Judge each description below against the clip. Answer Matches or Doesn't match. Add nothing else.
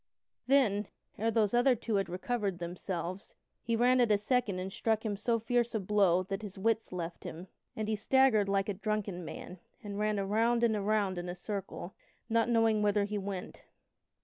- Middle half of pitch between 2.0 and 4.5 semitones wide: Matches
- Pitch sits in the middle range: Doesn't match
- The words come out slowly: Doesn't match